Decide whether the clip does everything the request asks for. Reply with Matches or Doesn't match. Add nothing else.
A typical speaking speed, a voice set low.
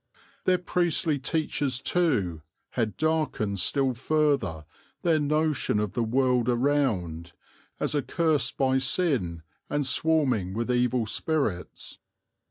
Doesn't match